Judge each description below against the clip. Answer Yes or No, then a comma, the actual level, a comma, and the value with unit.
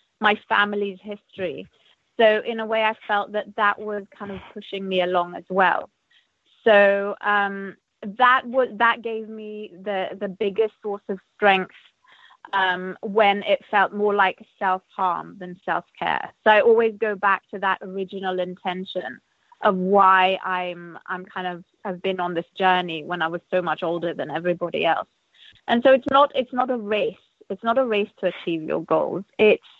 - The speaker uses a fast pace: No, average, 180 wpm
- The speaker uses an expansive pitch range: No, average, 2.8 semitones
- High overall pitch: Yes, high, 200 Hz